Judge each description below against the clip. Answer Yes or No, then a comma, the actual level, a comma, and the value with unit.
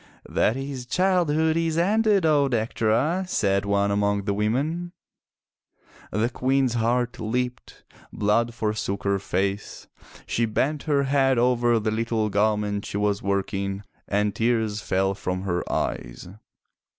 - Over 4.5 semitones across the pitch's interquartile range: Yes, average, 4.9 semitones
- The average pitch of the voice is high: No, low, 115 Hz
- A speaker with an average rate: No, slow, 130 wpm